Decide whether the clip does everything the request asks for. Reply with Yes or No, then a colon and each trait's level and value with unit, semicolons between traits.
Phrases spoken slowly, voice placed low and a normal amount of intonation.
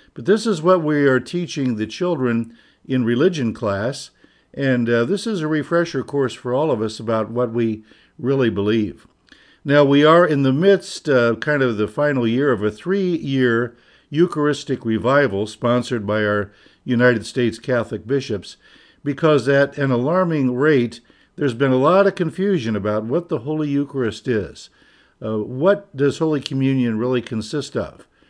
No: average, 170 wpm; low, 130 Hz; average, 4.5 semitones